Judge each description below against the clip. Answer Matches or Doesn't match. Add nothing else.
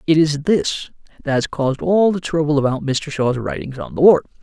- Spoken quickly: Matches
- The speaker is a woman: Doesn't match